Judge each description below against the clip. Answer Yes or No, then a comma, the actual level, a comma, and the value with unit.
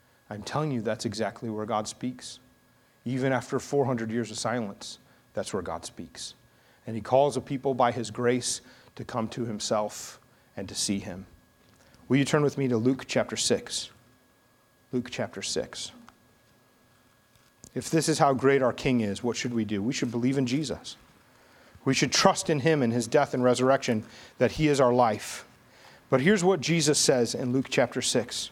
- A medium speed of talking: Yes, average, 185 wpm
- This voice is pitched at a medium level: No, low, 125 Hz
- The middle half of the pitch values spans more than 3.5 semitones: No, average, 3.2 semitones